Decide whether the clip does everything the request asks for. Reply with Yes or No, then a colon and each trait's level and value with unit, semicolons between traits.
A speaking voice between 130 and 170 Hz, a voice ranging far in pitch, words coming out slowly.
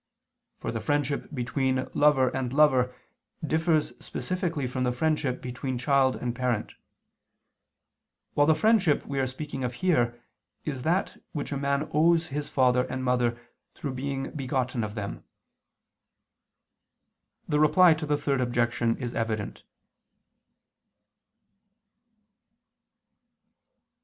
No: low, 135 Hz; average, 3.1 semitones; slow, 115 wpm